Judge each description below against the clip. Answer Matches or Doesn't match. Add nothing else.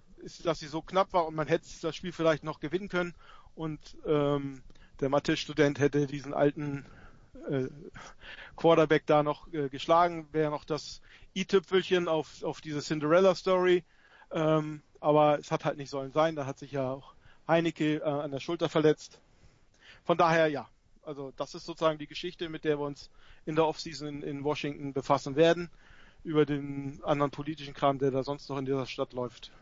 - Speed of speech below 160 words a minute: Doesn't match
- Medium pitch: Matches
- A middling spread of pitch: Doesn't match